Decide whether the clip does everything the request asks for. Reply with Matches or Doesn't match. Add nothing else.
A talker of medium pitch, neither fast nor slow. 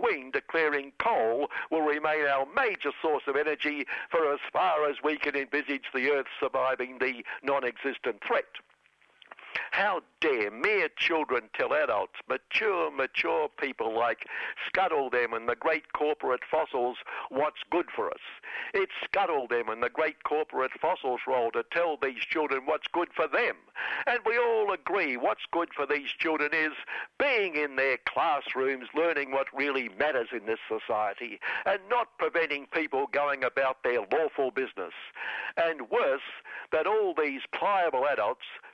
Matches